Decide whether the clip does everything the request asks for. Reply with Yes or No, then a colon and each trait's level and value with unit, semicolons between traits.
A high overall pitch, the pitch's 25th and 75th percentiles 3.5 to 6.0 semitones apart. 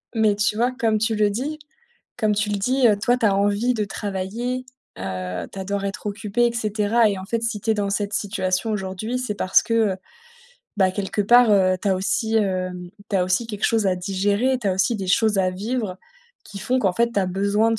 No: high, 205 Hz; average, 2.9 semitones